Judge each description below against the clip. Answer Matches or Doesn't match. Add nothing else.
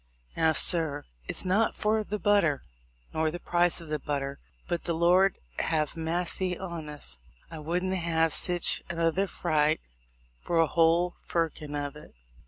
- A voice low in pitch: Doesn't match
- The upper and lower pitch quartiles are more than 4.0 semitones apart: Doesn't match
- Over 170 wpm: Doesn't match